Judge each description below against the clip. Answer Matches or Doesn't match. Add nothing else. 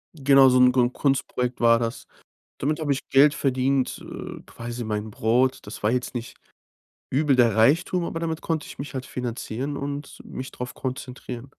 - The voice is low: Matches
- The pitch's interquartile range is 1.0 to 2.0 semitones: Doesn't match